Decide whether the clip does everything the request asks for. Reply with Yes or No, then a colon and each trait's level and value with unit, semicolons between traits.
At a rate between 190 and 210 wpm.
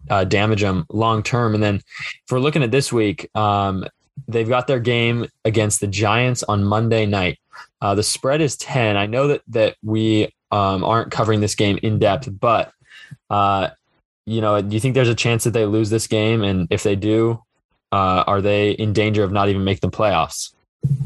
Yes: average, 200 wpm